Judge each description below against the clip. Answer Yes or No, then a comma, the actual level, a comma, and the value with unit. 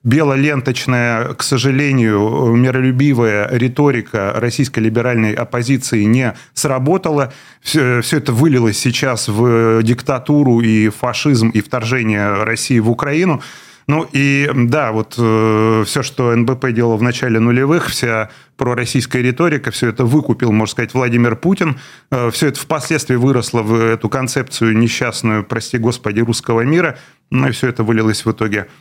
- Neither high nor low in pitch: No, low, 125 Hz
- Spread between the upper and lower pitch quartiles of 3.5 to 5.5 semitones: No, average, 3.1 semitones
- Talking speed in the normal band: Yes, average, 135 wpm